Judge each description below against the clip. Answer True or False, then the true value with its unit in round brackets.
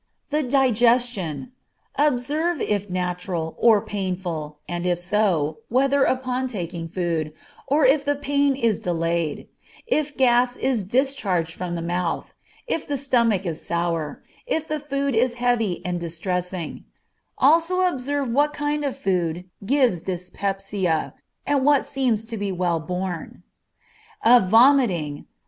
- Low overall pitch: False (215 Hz)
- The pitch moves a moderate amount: False (7.4 semitones)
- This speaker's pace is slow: True (130 wpm)